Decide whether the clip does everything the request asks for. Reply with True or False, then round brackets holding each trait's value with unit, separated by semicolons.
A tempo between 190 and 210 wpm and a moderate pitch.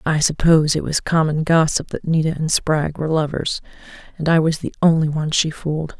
True (200 wpm; 155 Hz)